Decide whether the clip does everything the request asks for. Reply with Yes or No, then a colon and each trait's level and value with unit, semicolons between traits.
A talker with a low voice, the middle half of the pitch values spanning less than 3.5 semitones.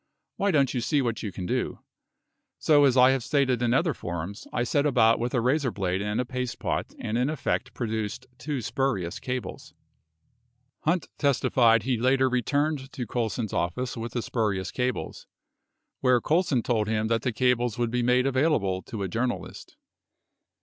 Yes: low, 125 Hz; average, 3.1 semitones